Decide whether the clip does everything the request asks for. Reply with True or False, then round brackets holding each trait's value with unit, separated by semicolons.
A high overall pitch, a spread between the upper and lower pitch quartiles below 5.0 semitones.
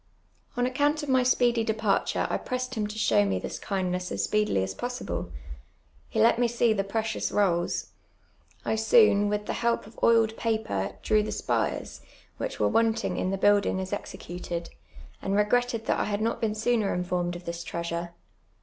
True (210 Hz; 4.2 semitones)